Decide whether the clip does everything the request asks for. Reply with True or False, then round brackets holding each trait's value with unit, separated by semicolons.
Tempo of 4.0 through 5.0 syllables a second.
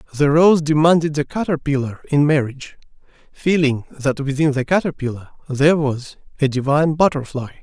False (5.5 syllables/s)